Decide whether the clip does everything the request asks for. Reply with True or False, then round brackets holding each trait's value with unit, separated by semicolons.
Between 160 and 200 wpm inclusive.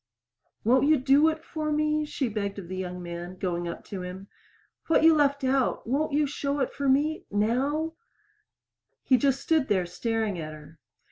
True (185 wpm)